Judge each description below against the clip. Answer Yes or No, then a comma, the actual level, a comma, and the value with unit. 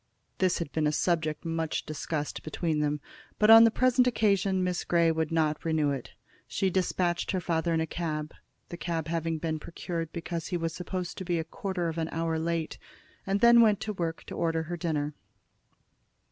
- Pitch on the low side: No, medium, 165 Hz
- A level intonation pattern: Yes, narrow, 2.2 semitones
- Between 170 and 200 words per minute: Yes, average, 195 wpm